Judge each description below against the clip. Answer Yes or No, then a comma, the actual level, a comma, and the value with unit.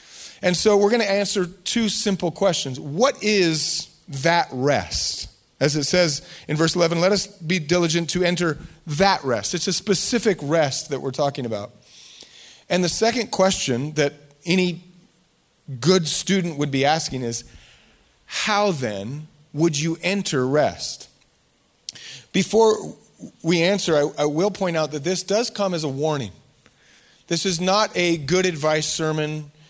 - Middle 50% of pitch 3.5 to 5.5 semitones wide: Yes, average, 4.2 semitones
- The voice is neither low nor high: Yes, medium, 170 Hz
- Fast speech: No, average, 150 wpm